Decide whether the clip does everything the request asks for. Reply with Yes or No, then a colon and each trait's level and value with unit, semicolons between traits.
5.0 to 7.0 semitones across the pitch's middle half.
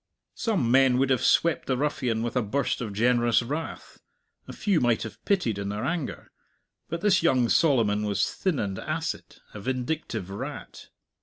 Yes: wide, 5.5 semitones